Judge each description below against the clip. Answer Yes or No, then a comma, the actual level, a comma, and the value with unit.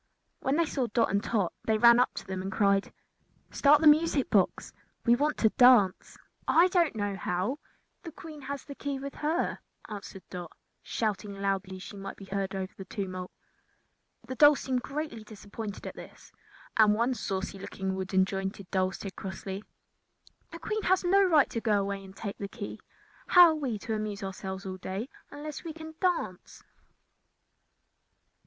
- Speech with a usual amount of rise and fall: No, wide, 6.7 semitones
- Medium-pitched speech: No, high, 215 Hz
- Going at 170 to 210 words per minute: Yes, average, 180 wpm